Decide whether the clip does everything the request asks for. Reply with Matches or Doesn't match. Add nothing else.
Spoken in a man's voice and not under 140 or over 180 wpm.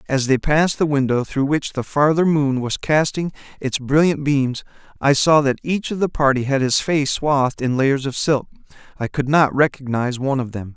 Doesn't match